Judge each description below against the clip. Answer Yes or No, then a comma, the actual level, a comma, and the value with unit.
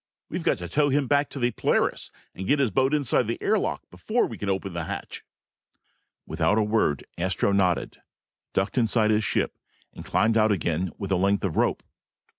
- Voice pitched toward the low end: Yes, low, 110 Hz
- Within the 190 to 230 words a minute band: Yes, average, 200 wpm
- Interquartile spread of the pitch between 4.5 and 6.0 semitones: Yes, wide, 5.6 semitones